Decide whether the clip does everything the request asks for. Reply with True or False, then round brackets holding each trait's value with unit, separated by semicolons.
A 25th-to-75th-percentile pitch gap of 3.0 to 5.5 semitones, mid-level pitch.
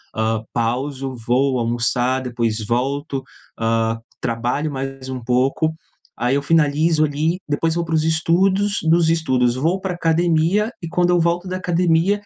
True (5.2 semitones; 145 Hz)